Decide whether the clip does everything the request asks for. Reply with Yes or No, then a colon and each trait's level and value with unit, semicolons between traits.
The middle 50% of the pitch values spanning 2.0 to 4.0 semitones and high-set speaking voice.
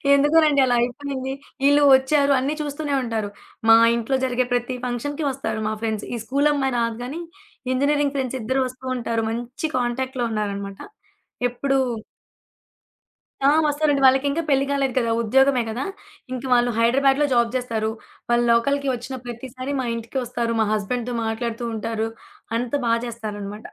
Yes: average, 3.0 semitones; very high, 250 Hz